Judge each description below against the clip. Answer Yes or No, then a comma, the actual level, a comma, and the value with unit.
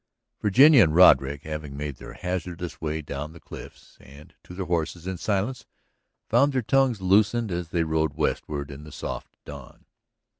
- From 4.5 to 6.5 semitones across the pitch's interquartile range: Yes, average, 4.9 semitones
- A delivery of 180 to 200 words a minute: No, average, 165 wpm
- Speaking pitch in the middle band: No, very low, 85 Hz